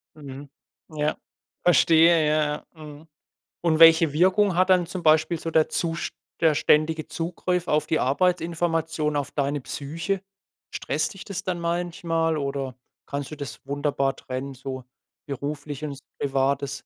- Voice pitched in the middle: Yes, medium, 155 Hz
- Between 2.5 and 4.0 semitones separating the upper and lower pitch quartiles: Yes, average, 2.9 semitones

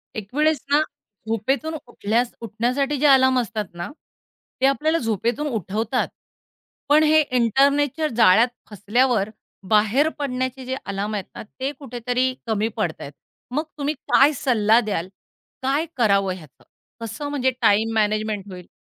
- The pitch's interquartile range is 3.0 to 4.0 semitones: No, average, 4.5 semitones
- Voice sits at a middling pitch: No, high, 240 Hz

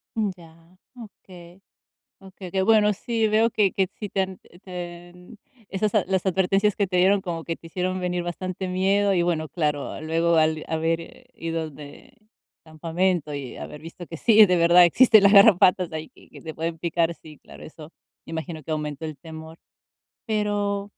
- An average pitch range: Yes, average, 3.2 semitones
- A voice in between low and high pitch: Yes, medium, 180 Hz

